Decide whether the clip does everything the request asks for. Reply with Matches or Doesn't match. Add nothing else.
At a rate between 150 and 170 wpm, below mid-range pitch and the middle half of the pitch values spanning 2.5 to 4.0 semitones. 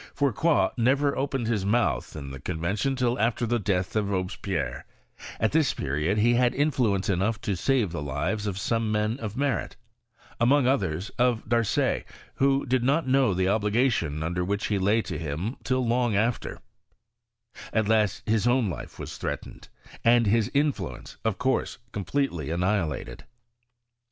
Doesn't match